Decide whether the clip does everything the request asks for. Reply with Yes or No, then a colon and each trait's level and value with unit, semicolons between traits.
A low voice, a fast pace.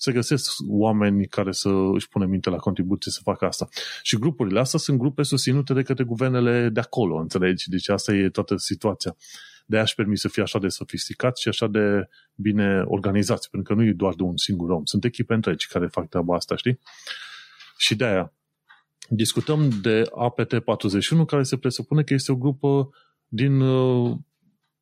Yes: low, 110 Hz; fast, 180 wpm